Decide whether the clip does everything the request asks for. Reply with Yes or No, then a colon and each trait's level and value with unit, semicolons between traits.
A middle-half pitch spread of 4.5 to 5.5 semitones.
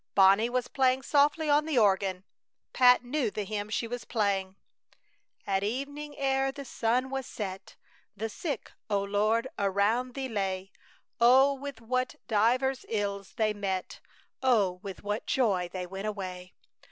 Yes: average, 4.8 semitones